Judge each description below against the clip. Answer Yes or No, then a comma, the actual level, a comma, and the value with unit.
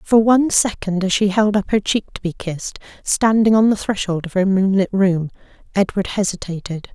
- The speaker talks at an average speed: Yes, average, 190 wpm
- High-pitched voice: Yes, high, 195 Hz